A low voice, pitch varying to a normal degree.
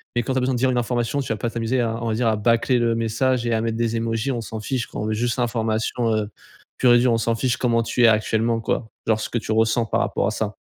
No: low, 115 Hz; narrow, 1.4 semitones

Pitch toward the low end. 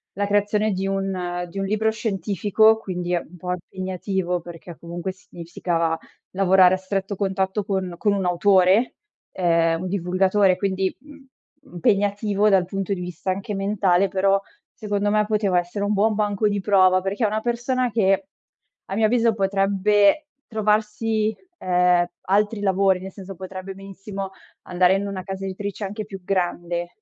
No: high, 195 Hz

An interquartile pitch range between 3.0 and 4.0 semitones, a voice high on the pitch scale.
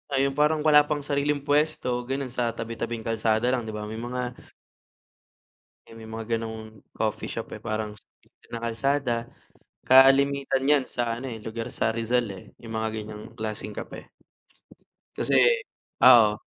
No: average, 3.4 semitones; low, 115 Hz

